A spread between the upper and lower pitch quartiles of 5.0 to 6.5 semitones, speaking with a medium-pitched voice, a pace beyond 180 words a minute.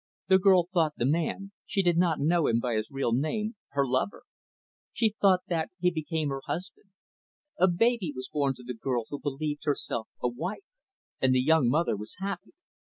Yes: wide, 5.6 semitones; medium, 155 Hz; average, 190 wpm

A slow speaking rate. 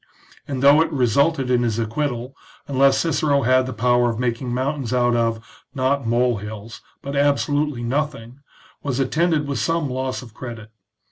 No: average, 160 wpm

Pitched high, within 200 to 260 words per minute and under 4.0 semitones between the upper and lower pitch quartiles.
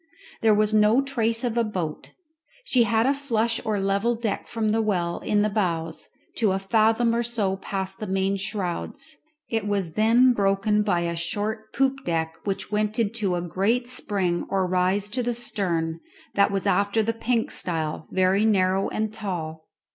No: high, 210 Hz; average, 175 wpm; average, 3.3 semitones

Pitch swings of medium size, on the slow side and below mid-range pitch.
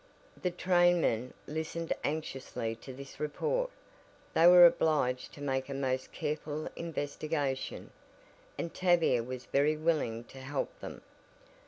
No: average, 3.9 semitones; slow, 125 wpm; medium, 150 Hz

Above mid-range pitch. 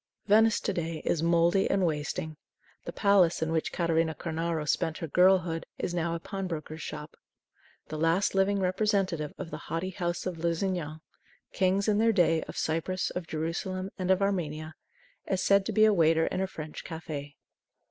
No: medium, 170 Hz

